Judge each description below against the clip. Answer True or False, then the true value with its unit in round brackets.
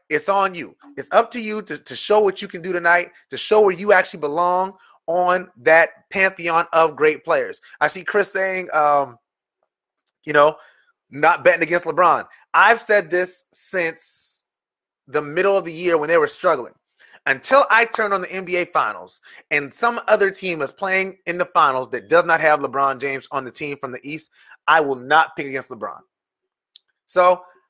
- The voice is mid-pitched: True (180 Hz)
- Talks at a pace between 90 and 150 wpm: False (185 wpm)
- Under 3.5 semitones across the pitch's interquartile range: False (4.3 semitones)